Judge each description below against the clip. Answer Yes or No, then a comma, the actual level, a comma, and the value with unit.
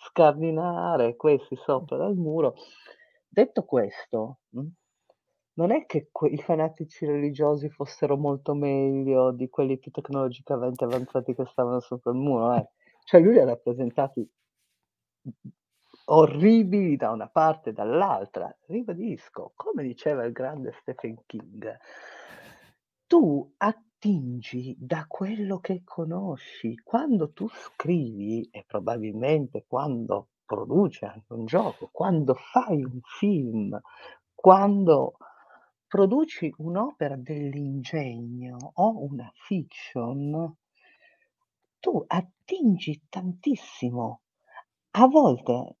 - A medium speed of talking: No, slow, 100 wpm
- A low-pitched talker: No, medium, 150 Hz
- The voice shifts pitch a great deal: Yes, wide, 6.5 semitones